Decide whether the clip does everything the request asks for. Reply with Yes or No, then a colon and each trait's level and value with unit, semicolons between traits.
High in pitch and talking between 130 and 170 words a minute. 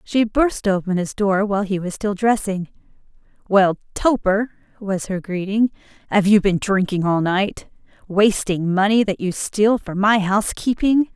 Yes: high, 200 Hz; average, 155 wpm